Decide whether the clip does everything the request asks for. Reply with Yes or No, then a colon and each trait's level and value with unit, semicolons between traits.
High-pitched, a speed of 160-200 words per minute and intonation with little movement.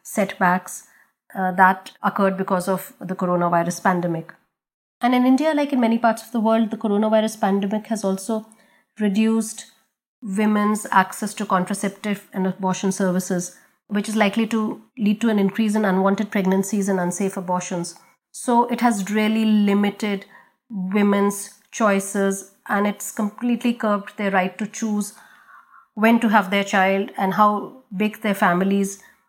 No: high, 205 Hz; average, 145 wpm; narrow, 2.3 semitones